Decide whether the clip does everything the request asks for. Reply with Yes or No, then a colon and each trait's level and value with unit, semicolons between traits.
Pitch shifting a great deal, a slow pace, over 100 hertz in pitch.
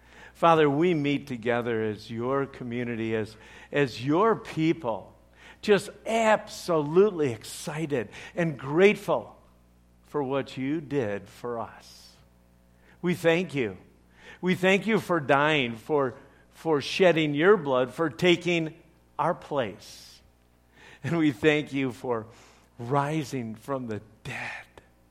Yes: wide, 6.9 semitones; slow, 115 wpm; low, 135 Hz